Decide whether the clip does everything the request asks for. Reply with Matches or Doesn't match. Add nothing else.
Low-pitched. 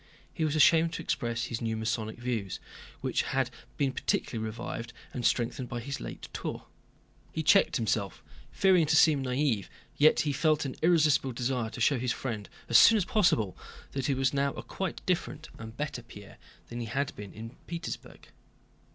Matches